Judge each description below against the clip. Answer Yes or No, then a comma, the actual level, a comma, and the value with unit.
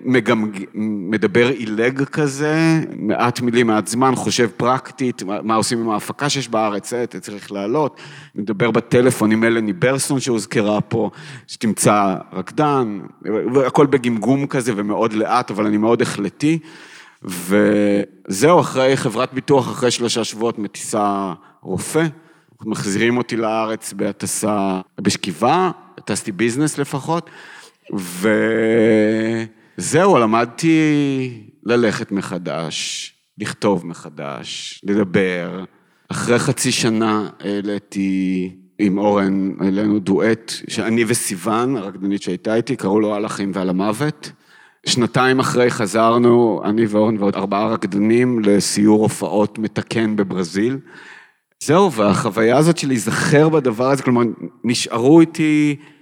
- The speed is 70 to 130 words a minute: Yes, average, 110 wpm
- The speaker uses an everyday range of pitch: Yes, average, 3.7 semitones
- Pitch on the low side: Yes, low, 115 Hz